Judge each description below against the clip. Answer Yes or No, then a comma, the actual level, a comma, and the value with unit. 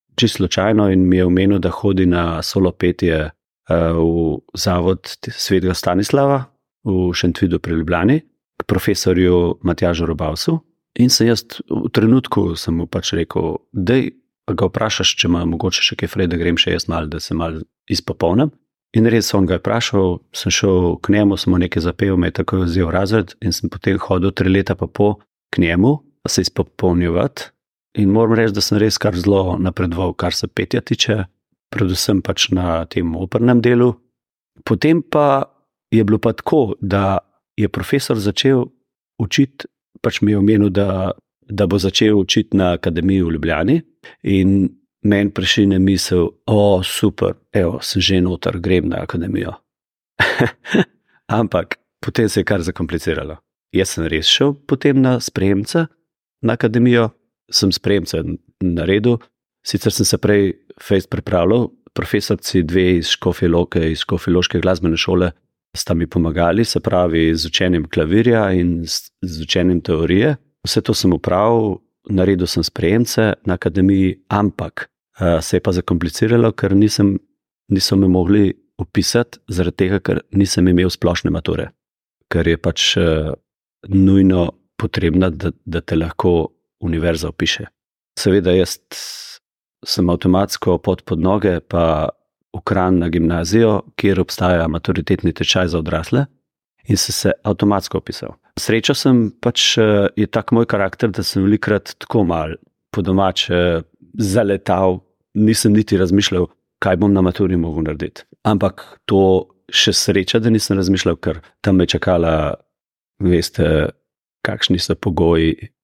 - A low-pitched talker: Yes, very low, 95 Hz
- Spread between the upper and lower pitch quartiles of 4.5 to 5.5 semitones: No, average, 3.5 semitones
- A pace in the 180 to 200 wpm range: No, average, 145 wpm